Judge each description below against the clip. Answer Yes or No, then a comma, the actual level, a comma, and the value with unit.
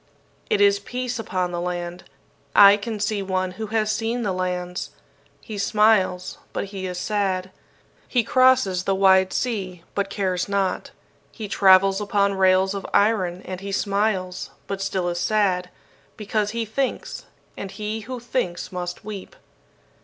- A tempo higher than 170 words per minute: No, average, 155 wpm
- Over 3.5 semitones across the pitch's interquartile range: No, narrow, 2.6 semitones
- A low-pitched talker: No, high, 195 Hz